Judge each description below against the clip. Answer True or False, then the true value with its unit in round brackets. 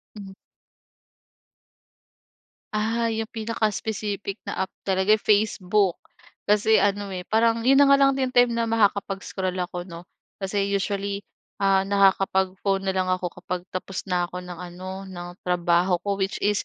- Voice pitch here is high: True (195 Hz)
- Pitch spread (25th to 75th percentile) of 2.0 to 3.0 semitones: True (2.5 semitones)